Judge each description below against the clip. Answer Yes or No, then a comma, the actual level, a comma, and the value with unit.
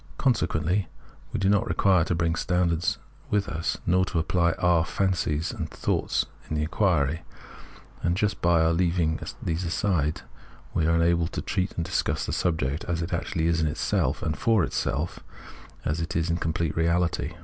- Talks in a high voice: No, very low, 85 Hz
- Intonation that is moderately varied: No, narrow, 2.0 semitones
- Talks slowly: No, average, 180 wpm